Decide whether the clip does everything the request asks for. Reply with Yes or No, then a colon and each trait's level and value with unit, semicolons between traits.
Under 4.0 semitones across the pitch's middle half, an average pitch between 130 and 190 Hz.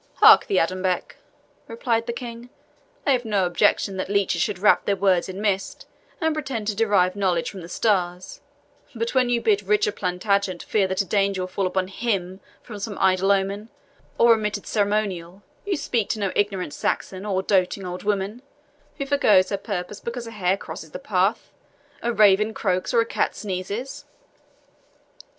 No: average, 3.2 semitones; high, 200 Hz